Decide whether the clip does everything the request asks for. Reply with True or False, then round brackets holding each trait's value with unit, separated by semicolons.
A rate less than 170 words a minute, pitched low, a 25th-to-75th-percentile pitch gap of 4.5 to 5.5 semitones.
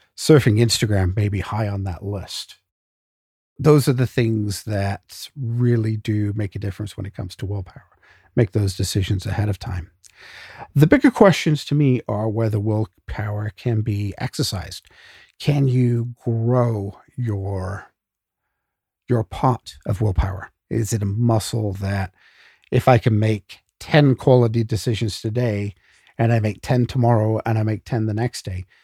False (150 wpm; 110 Hz; 3.3 semitones)